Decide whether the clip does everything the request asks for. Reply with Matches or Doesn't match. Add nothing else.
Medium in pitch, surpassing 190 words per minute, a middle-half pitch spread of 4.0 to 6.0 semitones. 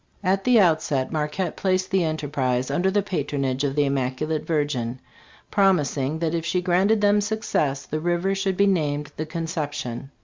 Doesn't match